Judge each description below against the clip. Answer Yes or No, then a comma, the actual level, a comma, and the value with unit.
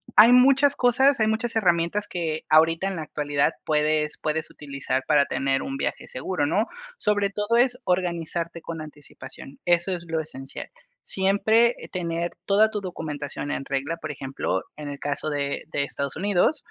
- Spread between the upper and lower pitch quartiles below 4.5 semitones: No, wide, 5.6 semitones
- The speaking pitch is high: No, medium, 165 Hz